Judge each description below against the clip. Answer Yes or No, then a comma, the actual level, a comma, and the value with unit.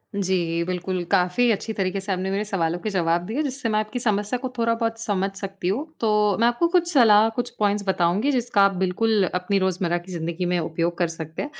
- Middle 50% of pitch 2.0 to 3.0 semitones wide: No, average, 4.0 semitones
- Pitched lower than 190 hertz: No, high, 195 Hz